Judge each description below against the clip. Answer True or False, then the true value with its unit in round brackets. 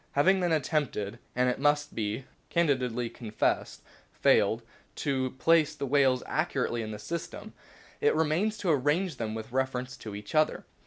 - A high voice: False (135 Hz)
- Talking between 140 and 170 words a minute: True (155 wpm)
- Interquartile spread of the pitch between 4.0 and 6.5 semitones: True (4.5 semitones)